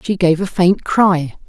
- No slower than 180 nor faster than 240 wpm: Yes, fast, 205 wpm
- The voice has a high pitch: No, medium, 180 Hz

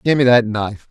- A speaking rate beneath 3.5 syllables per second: No, 6.2 syllables/s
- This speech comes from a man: Yes, male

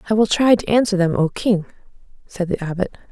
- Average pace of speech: No, fast, 210 wpm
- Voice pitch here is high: Yes, high, 195 Hz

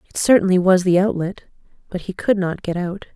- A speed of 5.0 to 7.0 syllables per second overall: Yes, 5.7 syllables/s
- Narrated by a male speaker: No, female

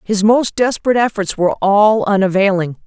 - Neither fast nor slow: Yes, average, 145 wpm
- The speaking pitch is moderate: No, high, 205 Hz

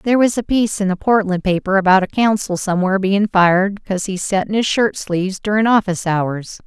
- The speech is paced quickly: Yes, fast, 215 wpm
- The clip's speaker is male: No, female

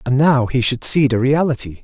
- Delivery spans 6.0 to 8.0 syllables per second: No, 5.2 syllables/s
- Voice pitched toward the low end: Yes, low, 130 Hz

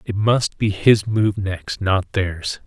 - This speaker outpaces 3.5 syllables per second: No, 3.1 syllables/s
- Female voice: No, male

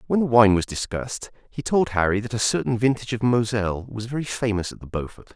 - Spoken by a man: Yes, male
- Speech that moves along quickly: Yes, fast, 225 wpm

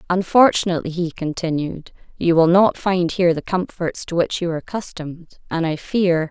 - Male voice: No, female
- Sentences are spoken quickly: No, average, 170 wpm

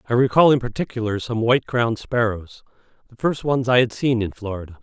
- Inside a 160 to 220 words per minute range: Yes, average, 200 wpm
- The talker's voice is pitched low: Yes, low, 115 Hz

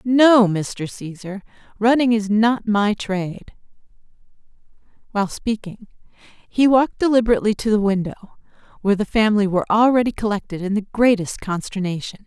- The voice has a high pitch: Yes, high, 210 Hz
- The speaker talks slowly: Yes, slow, 125 wpm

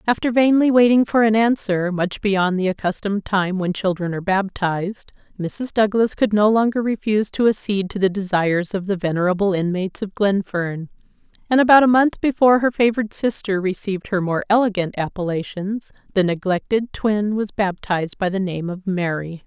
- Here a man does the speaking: No, female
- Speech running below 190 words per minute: Yes, average, 170 wpm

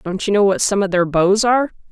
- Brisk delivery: Yes, fast, 285 wpm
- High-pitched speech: Yes, high, 200 Hz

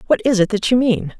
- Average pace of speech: No, fast, 300 wpm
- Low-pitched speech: No, high, 215 Hz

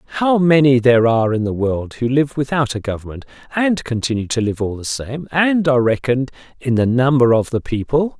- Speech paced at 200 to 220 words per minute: Yes, fast, 205 wpm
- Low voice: Yes, low, 130 Hz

